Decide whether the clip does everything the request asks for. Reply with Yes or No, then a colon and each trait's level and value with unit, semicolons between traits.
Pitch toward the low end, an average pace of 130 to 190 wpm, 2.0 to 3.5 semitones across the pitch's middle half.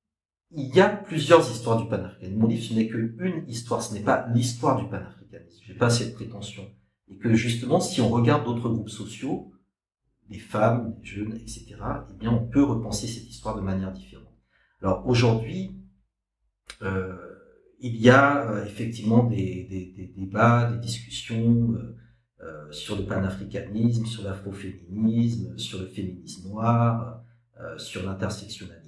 Yes: low, 115 Hz; average, 155 wpm; average, 2.7 semitones